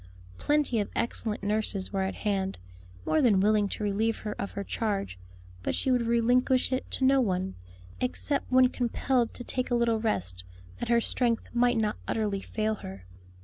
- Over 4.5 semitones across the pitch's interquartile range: No, average, 3.6 semitones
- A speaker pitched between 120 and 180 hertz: No, high, 225 Hz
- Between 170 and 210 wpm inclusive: Yes, average, 180 wpm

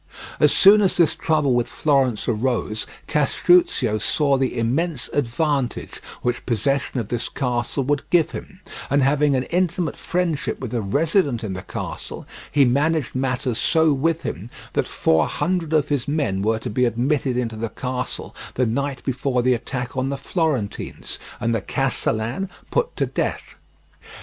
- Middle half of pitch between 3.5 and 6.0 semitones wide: Yes, average, 4.1 semitones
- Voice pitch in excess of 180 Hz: No, low, 135 Hz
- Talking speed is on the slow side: No, average, 160 wpm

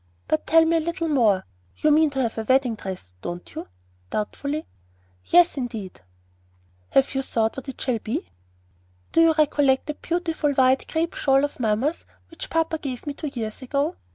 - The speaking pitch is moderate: No, very high, 275 Hz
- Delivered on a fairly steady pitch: No, average, 5.2 semitones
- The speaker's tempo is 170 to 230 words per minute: Yes, average, 180 wpm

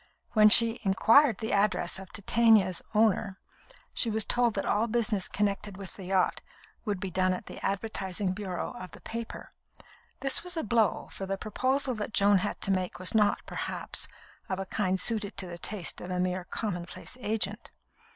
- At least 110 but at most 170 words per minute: No, average, 180 wpm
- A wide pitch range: No, average, 3.0 semitones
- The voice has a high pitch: Yes, high, 205 Hz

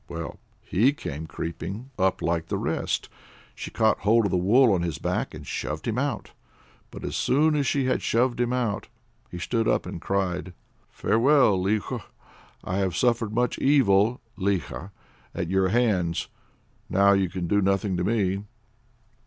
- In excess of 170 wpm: No, average, 165 wpm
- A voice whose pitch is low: Yes, low, 100 Hz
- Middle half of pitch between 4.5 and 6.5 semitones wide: Yes, average, 4.8 semitones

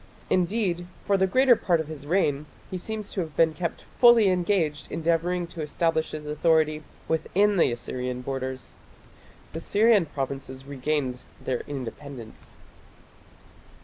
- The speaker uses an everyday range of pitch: Yes, average, 4.6 semitones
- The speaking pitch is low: No, medium, 160 Hz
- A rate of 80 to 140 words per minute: Yes, slow, 135 wpm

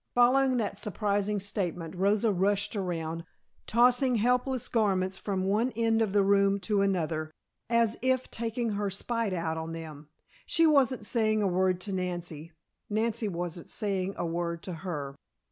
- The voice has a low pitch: No, high, 200 Hz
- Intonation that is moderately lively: Yes, average, 4.4 semitones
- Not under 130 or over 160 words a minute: Yes, average, 155 wpm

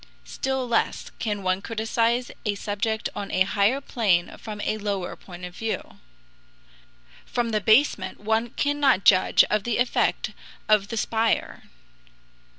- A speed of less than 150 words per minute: Yes, average, 140 wpm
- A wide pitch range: No, average, 2.8 semitones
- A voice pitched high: Yes, high, 220 Hz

